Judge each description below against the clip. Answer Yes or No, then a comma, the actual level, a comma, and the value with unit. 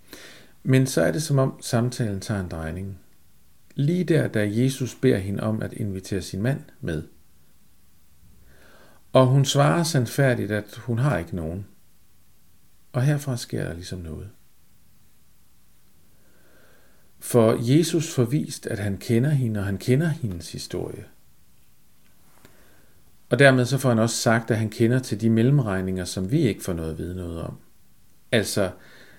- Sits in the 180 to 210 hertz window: No, low, 110 Hz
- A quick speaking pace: No, average, 150 wpm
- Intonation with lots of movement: Yes, wide, 6.1 semitones